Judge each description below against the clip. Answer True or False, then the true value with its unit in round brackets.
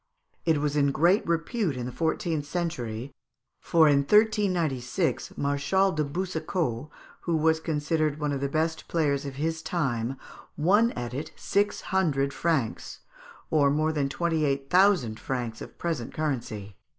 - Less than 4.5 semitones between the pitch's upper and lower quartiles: True (3.6 semitones)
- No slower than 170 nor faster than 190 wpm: False (150 wpm)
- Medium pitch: True (150 Hz)